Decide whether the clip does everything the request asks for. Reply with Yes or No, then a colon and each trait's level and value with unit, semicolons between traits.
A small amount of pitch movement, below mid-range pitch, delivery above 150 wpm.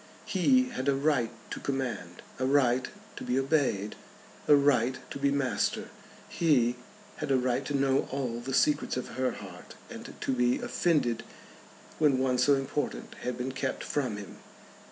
Yes: narrow, 2.3 semitones; low, 130 Hz; average, 165 wpm